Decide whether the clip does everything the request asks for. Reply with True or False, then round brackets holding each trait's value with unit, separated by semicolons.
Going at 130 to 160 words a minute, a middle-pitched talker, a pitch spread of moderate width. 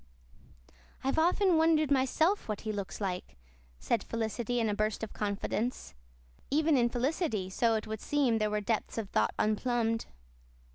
False (155 wpm; 230 Hz; 4.6 semitones)